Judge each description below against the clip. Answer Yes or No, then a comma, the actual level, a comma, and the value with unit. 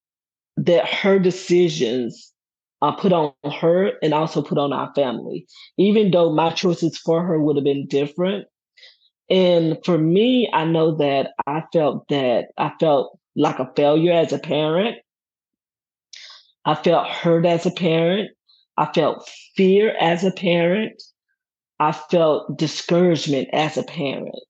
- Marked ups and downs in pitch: No, average, 3.3 semitones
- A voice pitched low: No, medium, 170 Hz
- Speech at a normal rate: Yes, average, 145 wpm